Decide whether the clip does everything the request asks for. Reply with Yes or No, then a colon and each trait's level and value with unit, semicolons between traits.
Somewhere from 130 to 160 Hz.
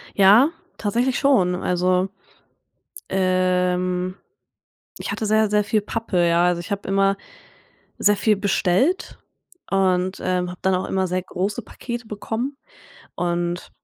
No: high, 190 Hz